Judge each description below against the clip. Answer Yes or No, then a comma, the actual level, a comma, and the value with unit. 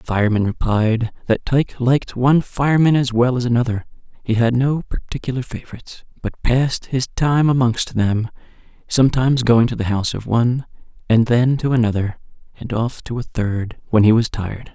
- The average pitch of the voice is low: Yes, low, 120 Hz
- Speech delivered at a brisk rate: No, average, 175 wpm